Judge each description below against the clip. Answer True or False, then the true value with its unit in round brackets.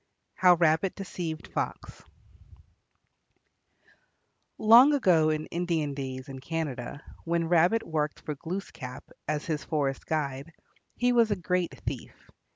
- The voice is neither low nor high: True (160 Hz)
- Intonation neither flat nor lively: True (3.5 semitones)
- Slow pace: True (120 wpm)